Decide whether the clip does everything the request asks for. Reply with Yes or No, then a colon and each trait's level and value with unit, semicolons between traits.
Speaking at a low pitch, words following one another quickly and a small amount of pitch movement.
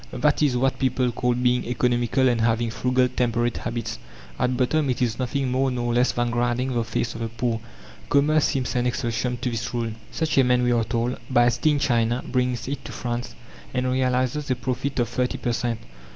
Yes: low, 125 Hz; fast, 210 wpm; narrow, 1.4 semitones